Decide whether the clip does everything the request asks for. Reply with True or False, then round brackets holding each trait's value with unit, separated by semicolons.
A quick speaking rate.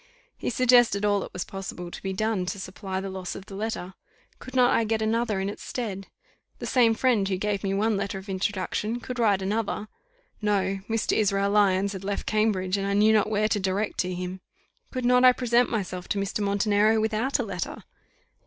True (210 wpm)